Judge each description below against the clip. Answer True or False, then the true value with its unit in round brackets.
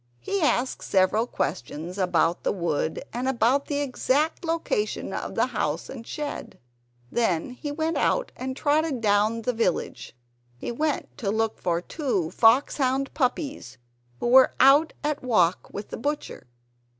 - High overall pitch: True (250 Hz)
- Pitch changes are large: True (6.1 semitones)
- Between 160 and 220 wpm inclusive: False (150 wpm)